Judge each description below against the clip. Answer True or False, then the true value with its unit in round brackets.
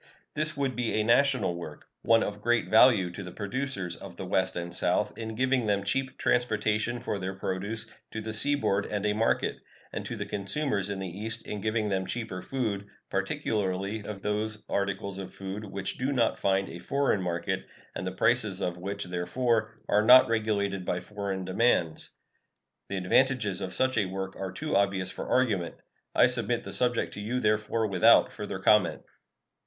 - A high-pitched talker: False (105 Hz)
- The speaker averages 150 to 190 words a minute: True (180 wpm)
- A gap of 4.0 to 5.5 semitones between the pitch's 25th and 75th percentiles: False (3.3 semitones)